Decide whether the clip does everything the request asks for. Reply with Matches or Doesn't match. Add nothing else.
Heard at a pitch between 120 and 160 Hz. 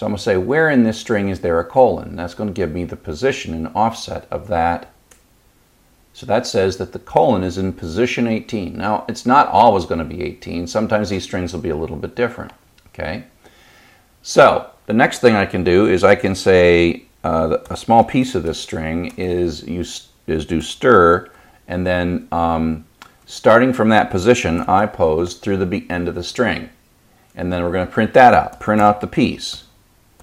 Doesn't match